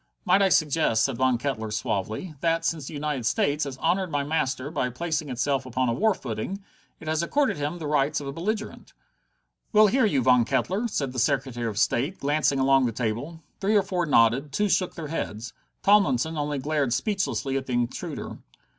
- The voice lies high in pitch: No, medium, 145 Hz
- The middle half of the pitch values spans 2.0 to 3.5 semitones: No, average, 4.7 semitones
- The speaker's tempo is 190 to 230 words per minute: Yes, average, 200 wpm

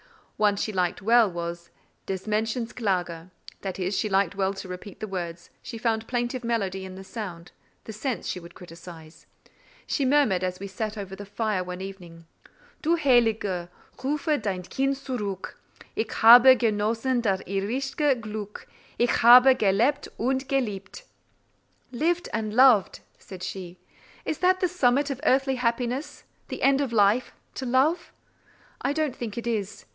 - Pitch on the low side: No, high, 220 Hz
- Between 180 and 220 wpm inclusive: No, average, 155 wpm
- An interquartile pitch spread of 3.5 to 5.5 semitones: Yes, average, 5.1 semitones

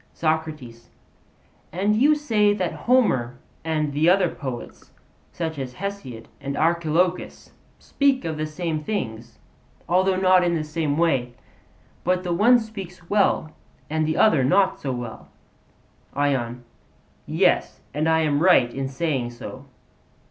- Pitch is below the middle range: No, medium, 160 Hz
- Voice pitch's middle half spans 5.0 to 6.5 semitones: Yes, wide, 5.5 semitones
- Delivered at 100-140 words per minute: Yes, slow, 135 wpm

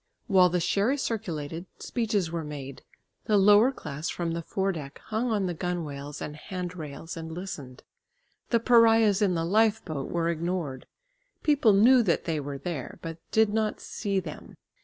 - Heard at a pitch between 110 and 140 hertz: No, medium, 180 Hz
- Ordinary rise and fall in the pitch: Yes, average, 5.0 semitones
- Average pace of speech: Yes, average, 165 wpm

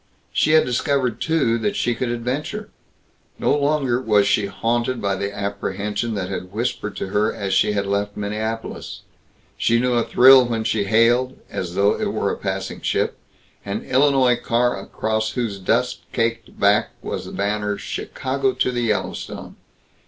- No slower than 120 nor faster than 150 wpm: No, average, 165 wpm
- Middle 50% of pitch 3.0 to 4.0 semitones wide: Yes, average, 3.7 semitones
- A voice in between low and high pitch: No, low, 115 Hz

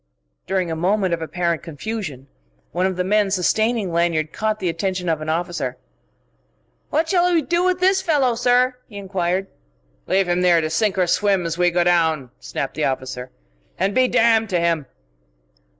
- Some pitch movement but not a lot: Yes, average, 4.7 semitones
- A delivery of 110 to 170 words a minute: No, average, 180 wpm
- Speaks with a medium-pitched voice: Yes, medium, 180 Hz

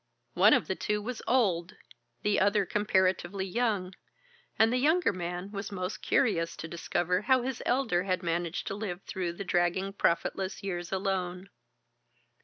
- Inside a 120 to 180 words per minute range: Yes, average, 155 wpm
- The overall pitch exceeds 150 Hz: Yes, high, 190 Hz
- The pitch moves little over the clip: No, average, 3.0 semitones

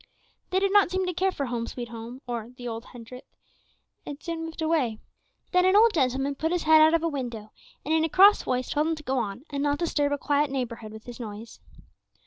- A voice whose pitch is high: Yes, very high, 285 Hz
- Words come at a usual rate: No, fast, 235 wpm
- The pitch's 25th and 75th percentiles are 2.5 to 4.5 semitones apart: No, average, 5.3 semitones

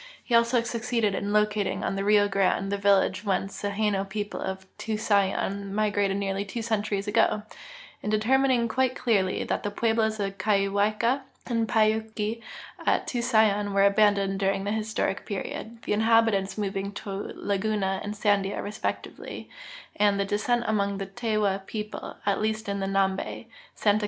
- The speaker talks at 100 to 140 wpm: No, average, 155 wpm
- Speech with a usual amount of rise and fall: No, narrow, 1.8 semitones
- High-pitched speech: Yes, high, 205 Hz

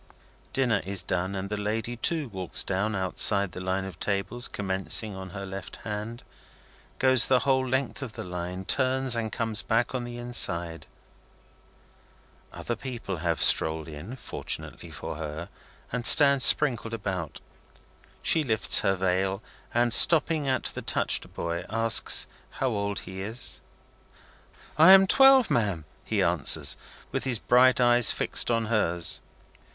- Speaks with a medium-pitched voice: No, low, 110 Hz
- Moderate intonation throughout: Yes, average, 4.7 semitones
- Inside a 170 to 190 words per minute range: No, average, 145 wpm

